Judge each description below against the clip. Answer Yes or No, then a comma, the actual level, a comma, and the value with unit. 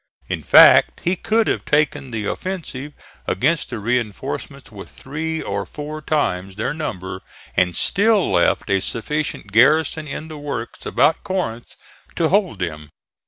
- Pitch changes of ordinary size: No, wide, 7.8 semitones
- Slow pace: No, average, 145 wpm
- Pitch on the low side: No, medium, 145 Hz